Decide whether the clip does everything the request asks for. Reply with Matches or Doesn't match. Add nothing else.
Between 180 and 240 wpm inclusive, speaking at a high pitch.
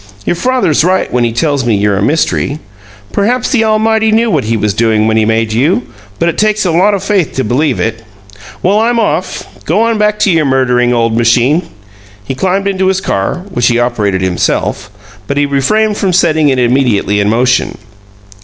Doesn't match